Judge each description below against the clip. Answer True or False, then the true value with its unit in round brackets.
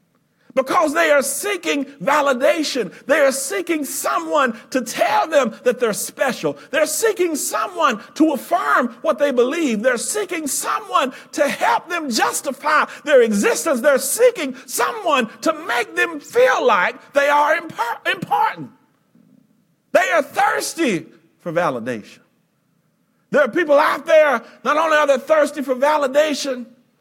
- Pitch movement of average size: True (3.2 semitones)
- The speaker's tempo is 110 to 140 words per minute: True (135 wpm)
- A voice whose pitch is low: False (290 Hz)